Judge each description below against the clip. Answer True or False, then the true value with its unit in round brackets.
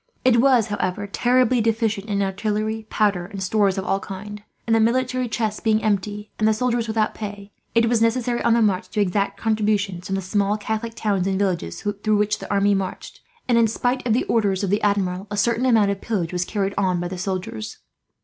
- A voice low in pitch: False (210 Hz)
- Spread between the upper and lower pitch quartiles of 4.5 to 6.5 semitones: False (2.5 semitones)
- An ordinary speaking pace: False (215 wpm)